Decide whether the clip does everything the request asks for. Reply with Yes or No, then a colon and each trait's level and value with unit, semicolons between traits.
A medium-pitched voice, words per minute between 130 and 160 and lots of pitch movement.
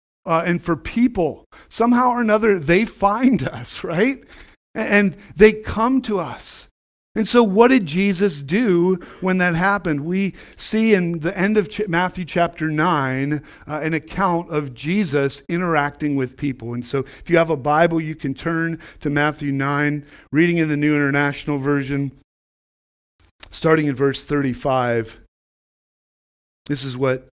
Yes: medium, 160 Hz; average, 150 wpm; wide, 5.7 semitones